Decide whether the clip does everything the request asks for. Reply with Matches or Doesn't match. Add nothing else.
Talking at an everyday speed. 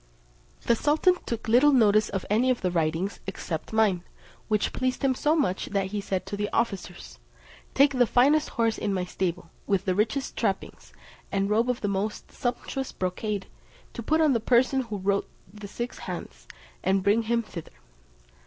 Matches